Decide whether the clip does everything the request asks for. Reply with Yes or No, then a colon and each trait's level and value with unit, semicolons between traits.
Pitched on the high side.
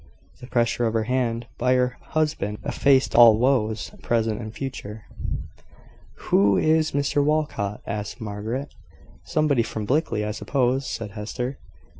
No: low, 120 Hz